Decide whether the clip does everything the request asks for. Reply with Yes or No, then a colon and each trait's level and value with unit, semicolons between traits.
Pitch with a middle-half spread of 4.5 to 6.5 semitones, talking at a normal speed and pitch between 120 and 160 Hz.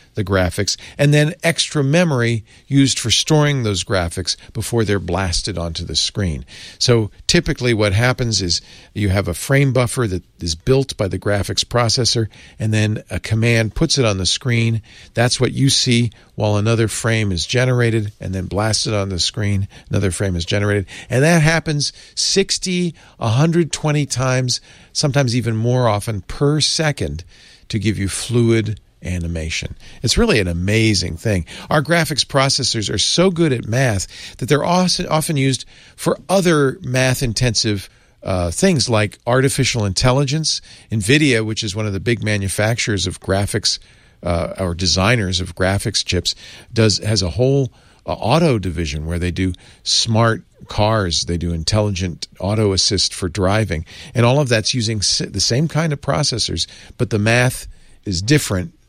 No: average, 5.1 semitones; average, 155 wpm; low, 110 Hz